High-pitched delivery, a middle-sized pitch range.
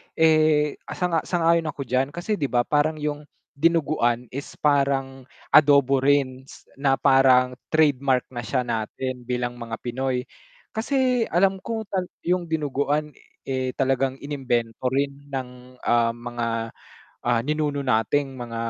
No: low, 135 Hz; average, 3.2 semitones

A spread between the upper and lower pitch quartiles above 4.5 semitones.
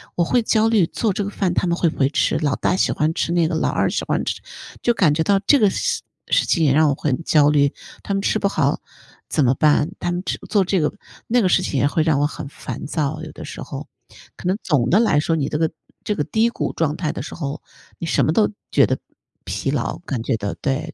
Yes: average, 5.0 semitones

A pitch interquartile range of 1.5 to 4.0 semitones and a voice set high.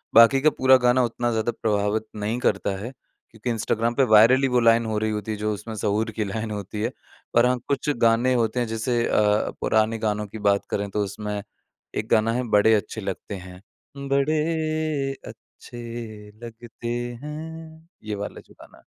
No: average, 3.1 semitones; low, 115 Hz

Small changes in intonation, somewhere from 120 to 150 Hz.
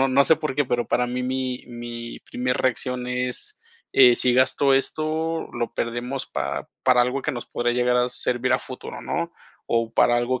Yes: narrow, 1.4 semitones; low, 125 Hz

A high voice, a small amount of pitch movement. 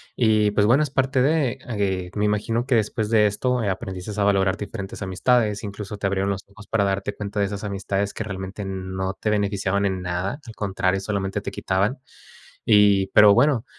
No: low, 100 Hz; narrow, 2.0 semitones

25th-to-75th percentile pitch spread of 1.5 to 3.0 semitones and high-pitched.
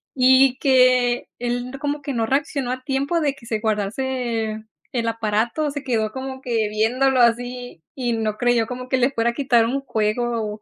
Yes: narrow, 2.6 semitones; high, 245 Hz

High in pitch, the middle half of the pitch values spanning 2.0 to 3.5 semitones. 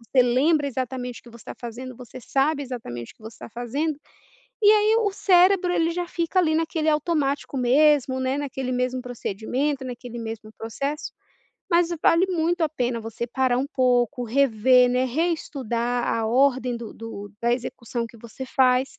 No: very high, 255 Hz; average, 4.1 semitones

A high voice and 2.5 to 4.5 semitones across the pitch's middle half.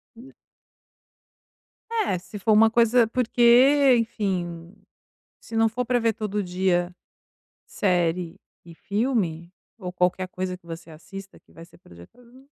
No: high, 195 Hz; average, 4.9 semitones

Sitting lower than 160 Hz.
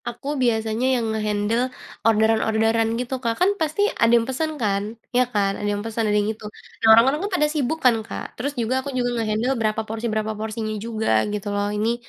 No: high, 225 Hz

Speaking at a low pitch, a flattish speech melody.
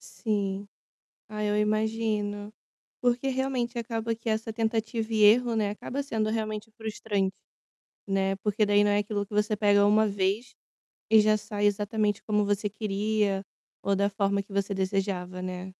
No: high, 210 Hz; narrow, 1.6 semitones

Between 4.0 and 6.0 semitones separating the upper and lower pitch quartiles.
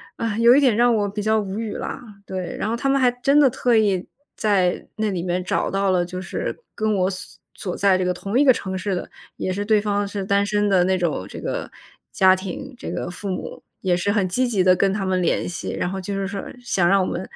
No: average, 2.8 semitones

